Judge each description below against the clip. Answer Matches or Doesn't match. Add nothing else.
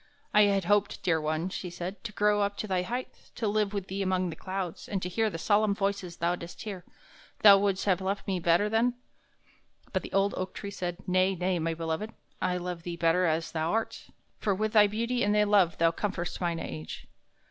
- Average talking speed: Doesn't match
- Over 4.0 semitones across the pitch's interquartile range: Doesn't match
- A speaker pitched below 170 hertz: Doesn't match